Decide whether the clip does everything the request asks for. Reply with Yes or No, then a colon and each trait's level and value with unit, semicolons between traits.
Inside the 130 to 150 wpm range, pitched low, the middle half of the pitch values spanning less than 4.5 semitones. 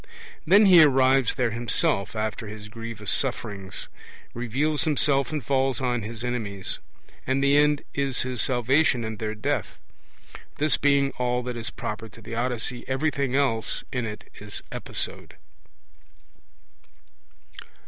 Yes: slow, 135 wpm; low, 125 Hz; average, 3.6 semitones